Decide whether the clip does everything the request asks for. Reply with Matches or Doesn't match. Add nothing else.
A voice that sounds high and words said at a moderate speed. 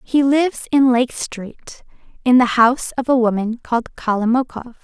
Matches